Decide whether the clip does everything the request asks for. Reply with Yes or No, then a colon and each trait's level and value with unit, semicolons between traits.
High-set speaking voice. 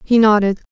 Yes: high, 215 Hz